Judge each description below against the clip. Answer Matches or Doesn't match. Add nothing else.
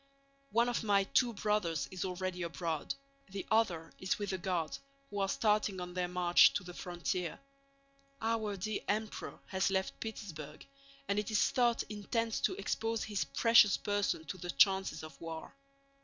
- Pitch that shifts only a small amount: Doesn't match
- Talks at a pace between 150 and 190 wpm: Matches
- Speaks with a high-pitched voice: Matches